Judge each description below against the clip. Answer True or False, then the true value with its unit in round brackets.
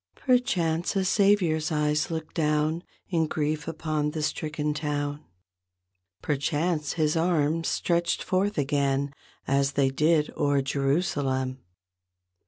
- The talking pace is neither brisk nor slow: False (110 wpm)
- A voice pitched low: False (150 Hz)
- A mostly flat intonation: True (2.3 semitones)